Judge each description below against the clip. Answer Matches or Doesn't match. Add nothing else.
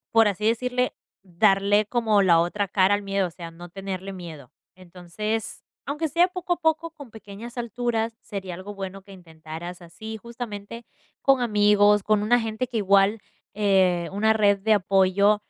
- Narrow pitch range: Doesn't match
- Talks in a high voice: Matches